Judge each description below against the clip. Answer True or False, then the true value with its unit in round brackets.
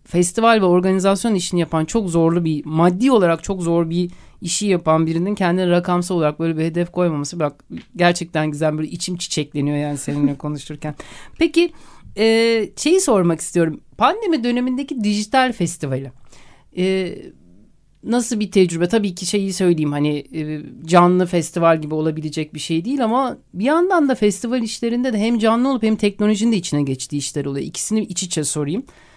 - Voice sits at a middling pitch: True (175 Hz)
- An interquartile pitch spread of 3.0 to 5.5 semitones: False (5.9 semitones)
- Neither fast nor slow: False (165 wpm)